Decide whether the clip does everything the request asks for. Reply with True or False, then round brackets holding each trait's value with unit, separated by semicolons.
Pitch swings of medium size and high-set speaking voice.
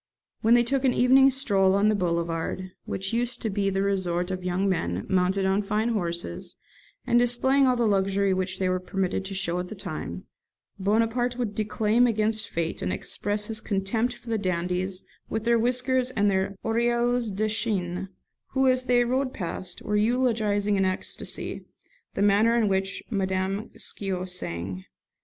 True (3.9 semitones; 205 Hz)